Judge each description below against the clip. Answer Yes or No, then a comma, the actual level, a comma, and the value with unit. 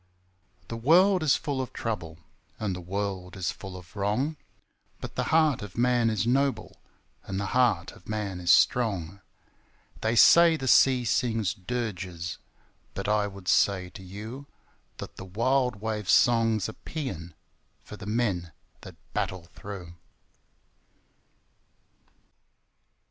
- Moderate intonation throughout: Yes, average, 4.8 semitones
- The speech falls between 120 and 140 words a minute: Yes, slow, 135 wpm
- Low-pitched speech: Yes, low, 105 Hz